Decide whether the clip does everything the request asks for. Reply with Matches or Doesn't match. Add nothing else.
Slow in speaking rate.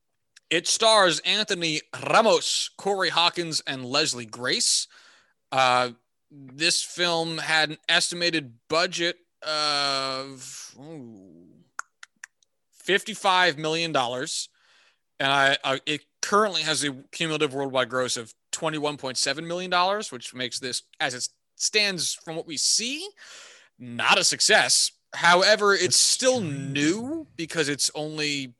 Matches